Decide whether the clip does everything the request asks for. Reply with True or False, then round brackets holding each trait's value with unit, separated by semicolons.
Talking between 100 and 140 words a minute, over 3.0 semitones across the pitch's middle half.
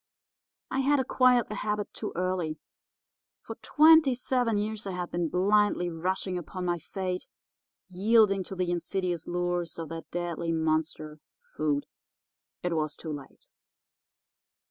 True (135 wpm; 3.9 semitones)